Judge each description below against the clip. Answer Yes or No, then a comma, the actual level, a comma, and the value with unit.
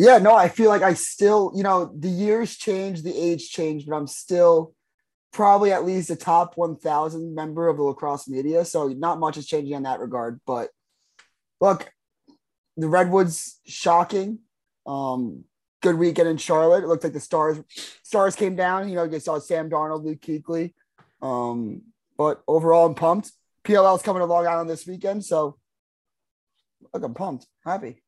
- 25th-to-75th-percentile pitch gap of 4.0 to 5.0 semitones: No, average, 3.6 semitones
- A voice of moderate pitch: Yes, medium, 170 Hz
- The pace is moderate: Yes, average, 175 wpm